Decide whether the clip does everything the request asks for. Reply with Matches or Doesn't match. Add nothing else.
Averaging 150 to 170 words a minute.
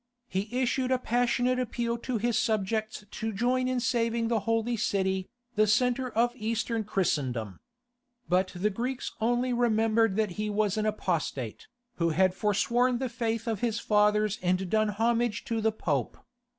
Matches